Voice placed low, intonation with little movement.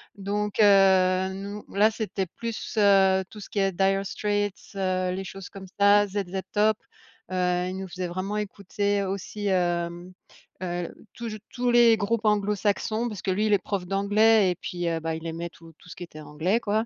No: high, 195 Hz; narrow, 2.1 semitones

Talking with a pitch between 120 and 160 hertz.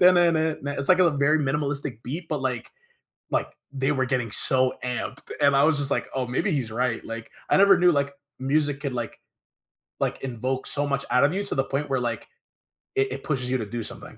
Yes: medium, 140 Hz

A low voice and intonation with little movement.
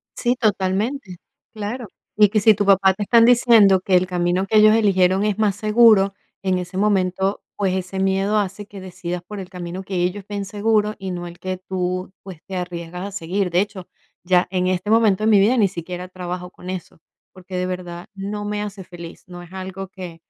No: high, 190 Hz; narrow, 2.3 semitones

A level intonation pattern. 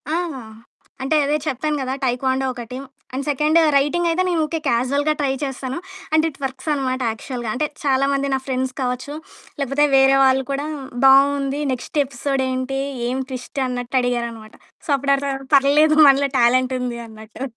Yes: narrow, 1.8 semitones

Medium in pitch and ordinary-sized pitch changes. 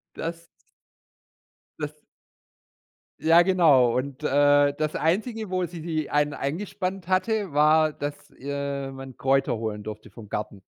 Yes: medium, 145 Hz; average, 4.0 semitones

